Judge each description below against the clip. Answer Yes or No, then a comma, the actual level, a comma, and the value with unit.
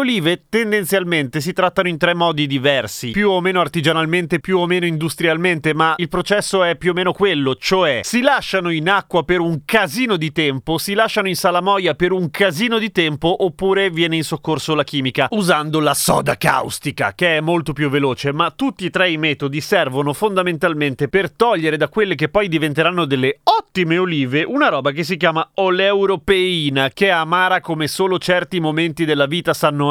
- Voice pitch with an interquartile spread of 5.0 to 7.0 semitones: No, average, 3.4 semitones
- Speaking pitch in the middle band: Yes, medium, 175 Hz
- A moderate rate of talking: No, fast, 185 wpm